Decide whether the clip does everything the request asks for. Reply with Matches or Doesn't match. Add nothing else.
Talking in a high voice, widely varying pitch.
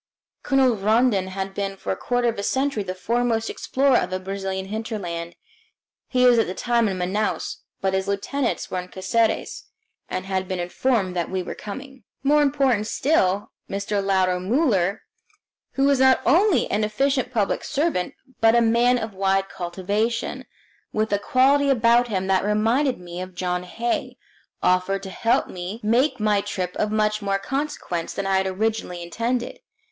Doesn't match